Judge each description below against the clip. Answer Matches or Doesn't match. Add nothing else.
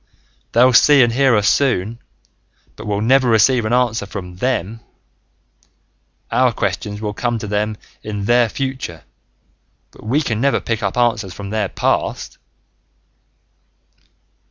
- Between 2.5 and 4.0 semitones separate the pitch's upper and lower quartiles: Matches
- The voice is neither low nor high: Doesn't match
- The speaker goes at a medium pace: Doesn't match